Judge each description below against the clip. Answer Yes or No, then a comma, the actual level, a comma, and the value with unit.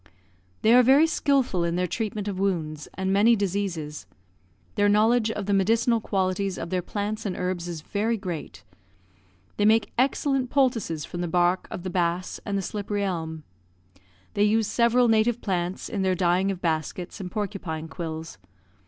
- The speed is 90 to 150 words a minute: No, average, 170 wpm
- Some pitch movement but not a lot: Yes, average, 3.8 semitones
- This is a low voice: No, high, 195 Hz